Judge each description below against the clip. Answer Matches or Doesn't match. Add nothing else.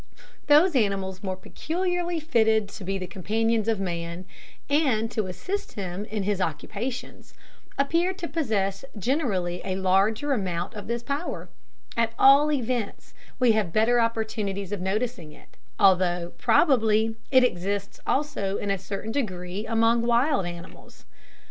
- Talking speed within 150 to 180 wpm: Doesn't match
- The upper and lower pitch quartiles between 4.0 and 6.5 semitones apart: Matches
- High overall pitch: Matches